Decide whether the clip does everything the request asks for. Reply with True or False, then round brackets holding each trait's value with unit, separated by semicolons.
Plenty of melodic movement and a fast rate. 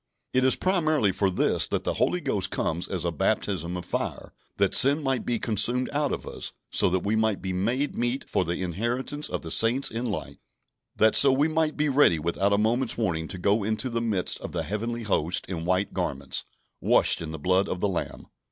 True (5.9 semitones; 215 wpm)